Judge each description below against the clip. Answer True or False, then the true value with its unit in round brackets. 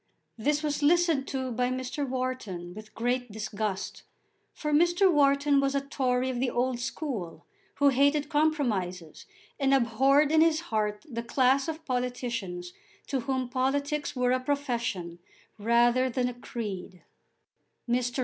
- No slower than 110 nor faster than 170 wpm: True (140 wpm)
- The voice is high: True (255 Hz)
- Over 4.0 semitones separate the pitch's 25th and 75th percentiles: False (3.4 semitones)